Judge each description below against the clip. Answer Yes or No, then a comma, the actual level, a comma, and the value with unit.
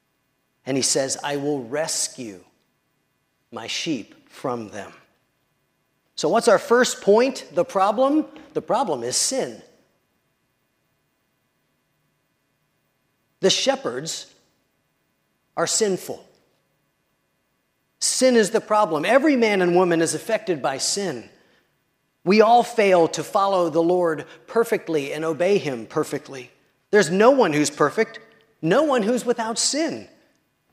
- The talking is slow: Yes, slow, 115 wpm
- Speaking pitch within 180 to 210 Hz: Yes, high, 190 Hz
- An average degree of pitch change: No, wide, 6.8 semitones